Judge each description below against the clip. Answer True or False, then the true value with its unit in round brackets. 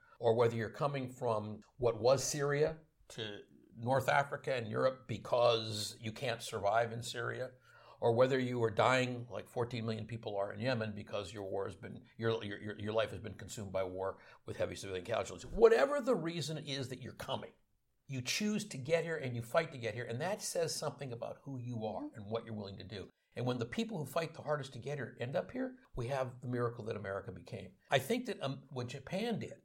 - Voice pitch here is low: True (120 Hz)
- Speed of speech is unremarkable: False (220 wpm)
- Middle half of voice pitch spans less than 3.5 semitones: False (4.2 semitones)